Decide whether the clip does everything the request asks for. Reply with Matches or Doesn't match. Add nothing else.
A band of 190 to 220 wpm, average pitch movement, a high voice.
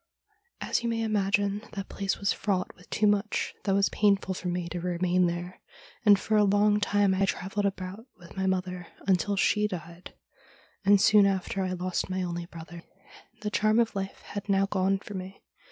Doesn't match